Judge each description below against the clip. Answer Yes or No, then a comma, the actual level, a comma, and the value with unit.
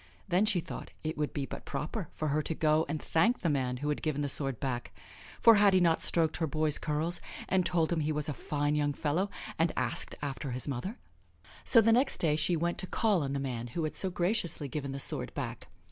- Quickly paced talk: Yes, fast, 240 wpm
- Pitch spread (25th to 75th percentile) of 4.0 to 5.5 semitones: No, average, 3.4 semitones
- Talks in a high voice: No, medium, 155 Hz